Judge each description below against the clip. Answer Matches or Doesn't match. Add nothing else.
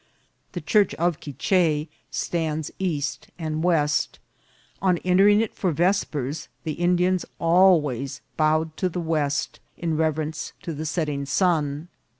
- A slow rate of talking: Matches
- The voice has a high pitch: Doesn't match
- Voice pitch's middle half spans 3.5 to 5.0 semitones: Doesn't match